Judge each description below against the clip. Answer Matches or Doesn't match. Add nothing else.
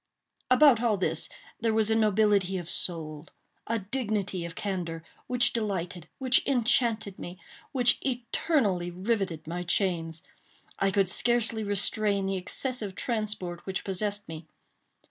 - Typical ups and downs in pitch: Matches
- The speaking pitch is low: Doesn't match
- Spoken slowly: Matches